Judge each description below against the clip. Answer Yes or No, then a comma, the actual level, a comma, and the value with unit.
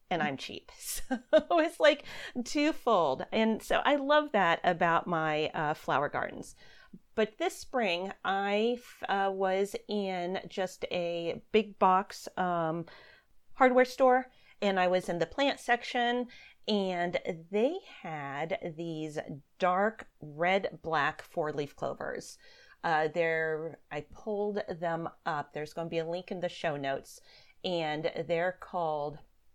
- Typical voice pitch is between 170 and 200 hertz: Yes, medium, 185 Hz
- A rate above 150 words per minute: No, slow, 135 wpm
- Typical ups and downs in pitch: No, wide, 6.1 semitones